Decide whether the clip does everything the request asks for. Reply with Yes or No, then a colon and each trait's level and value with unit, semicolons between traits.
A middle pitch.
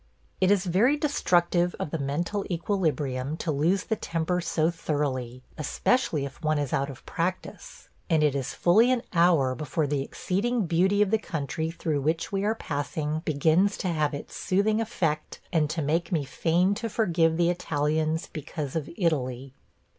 Yes: medium, 165 Hz